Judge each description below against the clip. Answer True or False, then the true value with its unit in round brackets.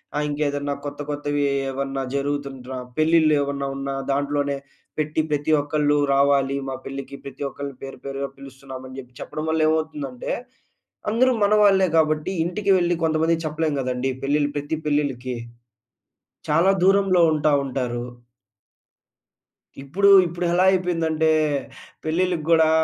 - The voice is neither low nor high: True (145 Hz)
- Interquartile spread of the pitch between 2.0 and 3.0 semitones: True (2.7 semitones)